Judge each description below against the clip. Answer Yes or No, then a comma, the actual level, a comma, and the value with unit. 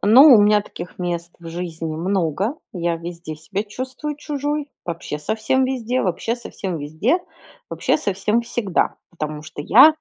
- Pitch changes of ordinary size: No, wide, 6.6 semitones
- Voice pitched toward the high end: Yes, high, 195 Hz